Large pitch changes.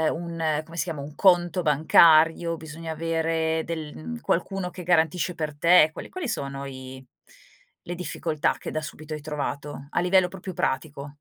No: narrow, 2.6 semitones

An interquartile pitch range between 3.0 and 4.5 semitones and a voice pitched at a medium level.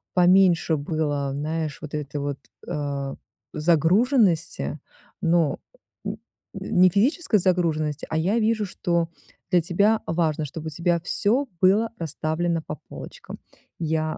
Yes: average, 3.3 semitones; medium, 165 Hz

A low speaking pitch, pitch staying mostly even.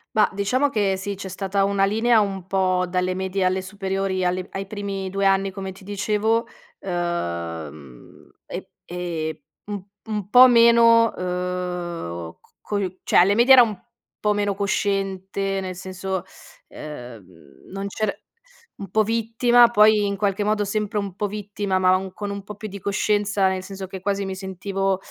No: high, 195 Hz; narrow, 1.9 semitones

